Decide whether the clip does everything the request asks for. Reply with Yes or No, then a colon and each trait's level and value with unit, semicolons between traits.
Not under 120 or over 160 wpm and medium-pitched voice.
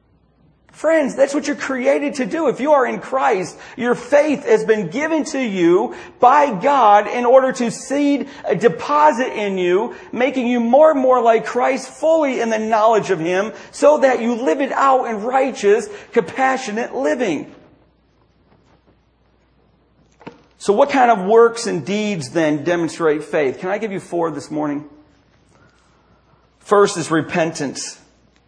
No: average, 150 wpm; high, 235 Hz